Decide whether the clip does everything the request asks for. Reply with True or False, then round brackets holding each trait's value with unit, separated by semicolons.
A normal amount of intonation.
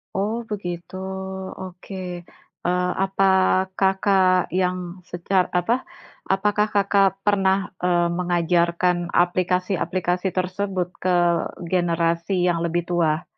False (1.8 semitones)